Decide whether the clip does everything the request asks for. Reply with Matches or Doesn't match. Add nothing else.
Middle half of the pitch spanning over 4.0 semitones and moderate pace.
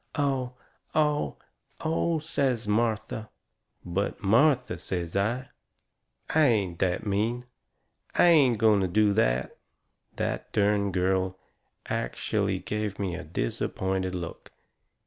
Doesn't match